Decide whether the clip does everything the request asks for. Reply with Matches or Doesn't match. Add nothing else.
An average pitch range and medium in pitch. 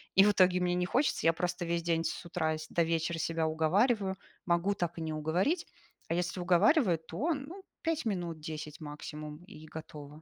Matches